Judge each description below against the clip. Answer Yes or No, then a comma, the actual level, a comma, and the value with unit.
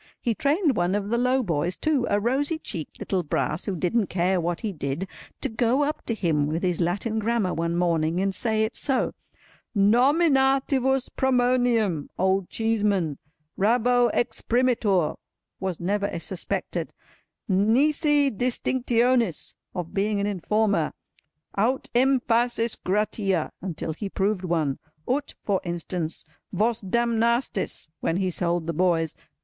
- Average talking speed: No, slow, 120 wpm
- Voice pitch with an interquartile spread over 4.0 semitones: Yes, wide, 5.6 semitones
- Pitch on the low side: No, high, 210 Hz